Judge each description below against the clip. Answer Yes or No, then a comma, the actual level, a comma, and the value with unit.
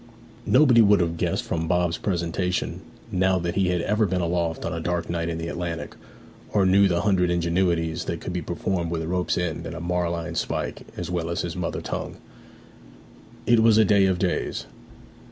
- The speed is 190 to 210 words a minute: Yes, average, 195 wpm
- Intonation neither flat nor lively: No, narrow, 1.9 semitones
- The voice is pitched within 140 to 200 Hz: No, very low, 90 Hz